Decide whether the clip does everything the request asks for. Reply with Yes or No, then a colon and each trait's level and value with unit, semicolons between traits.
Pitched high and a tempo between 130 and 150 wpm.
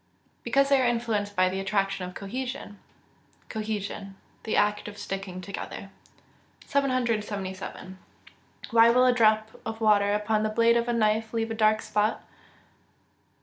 Yes: high, 215 Hz; average, 145 wpm